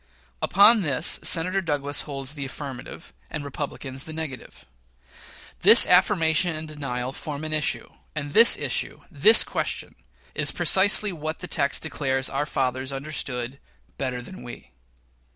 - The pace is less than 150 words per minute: Yes, slow, 135 wpm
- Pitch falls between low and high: Yes, medium, 145 Hz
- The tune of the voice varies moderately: Yes, average, 3.2 semitones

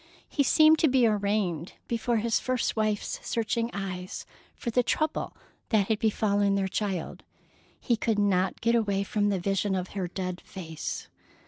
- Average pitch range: Yes, average, 3.2 semitones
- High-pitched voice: Yes, high, 205 Hz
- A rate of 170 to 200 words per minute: No, average, 160 wpm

